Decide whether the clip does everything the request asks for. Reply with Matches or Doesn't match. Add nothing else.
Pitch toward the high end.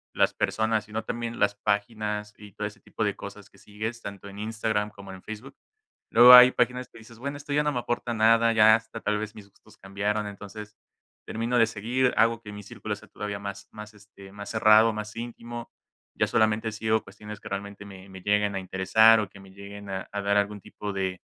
Doesn't match